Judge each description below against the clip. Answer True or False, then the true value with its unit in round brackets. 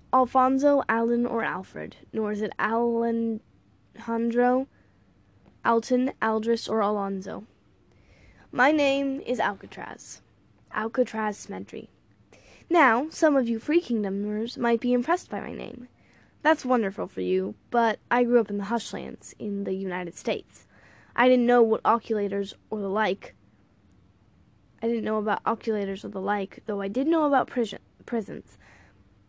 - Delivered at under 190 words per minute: True (140 wpm)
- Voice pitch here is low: False (225 Hz)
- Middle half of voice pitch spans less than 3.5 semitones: False (3.9 semitones)